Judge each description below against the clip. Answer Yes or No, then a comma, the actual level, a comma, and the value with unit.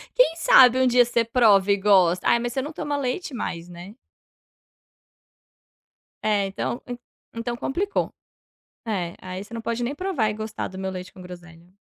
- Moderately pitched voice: No, high, 220 Hz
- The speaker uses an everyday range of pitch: Yes, average, 5.0 semitones